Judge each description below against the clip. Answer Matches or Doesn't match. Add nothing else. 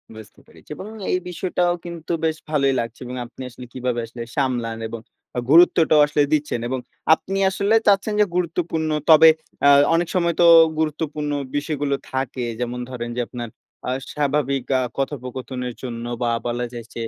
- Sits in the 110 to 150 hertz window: Matches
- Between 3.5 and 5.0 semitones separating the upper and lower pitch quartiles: Matches